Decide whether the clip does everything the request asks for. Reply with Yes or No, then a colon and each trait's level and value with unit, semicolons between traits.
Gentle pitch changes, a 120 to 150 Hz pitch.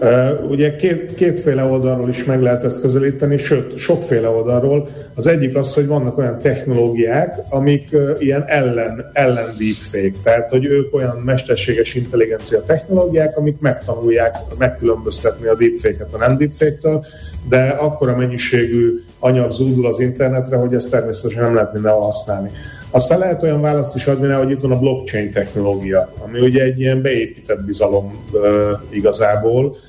No: average, 3.8 semitones; low, 130 Hz